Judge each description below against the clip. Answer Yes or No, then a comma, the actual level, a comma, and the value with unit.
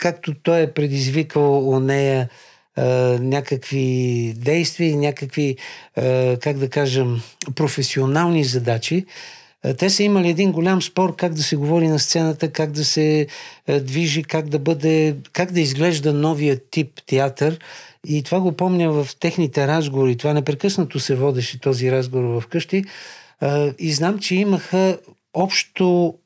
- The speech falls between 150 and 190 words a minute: No, average, 135 wpm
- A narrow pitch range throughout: No, average, 3.8 semitones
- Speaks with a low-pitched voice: No, medium, 150 Hz